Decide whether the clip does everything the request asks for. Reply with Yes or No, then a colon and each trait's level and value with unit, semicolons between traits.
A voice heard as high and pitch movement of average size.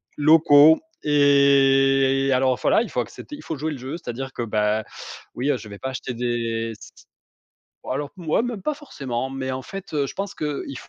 No: low, 135 Hz; average, 3.0 semitones